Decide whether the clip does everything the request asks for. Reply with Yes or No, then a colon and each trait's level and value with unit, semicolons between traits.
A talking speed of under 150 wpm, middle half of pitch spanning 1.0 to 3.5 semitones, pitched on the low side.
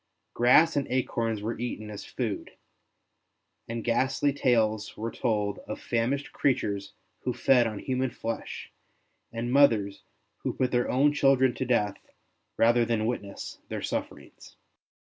Yes: slow, 135 wpm; average, 3.0 semitones; low, 120 Hz